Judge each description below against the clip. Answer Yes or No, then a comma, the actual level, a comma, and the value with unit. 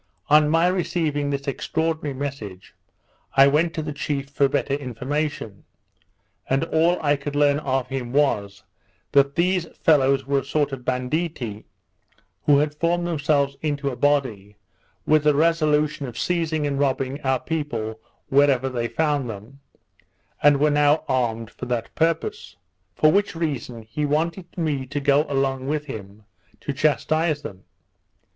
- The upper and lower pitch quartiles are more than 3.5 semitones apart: No, narrow, 2.6 semitones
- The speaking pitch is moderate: Yes, medium, 145 Hz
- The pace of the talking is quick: No, average, 150 wpm